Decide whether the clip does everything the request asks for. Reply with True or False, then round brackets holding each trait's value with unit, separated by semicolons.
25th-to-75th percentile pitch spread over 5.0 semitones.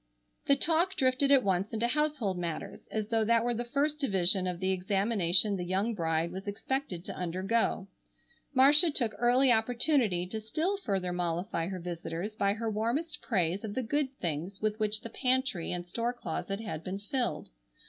True (5.6 semitones)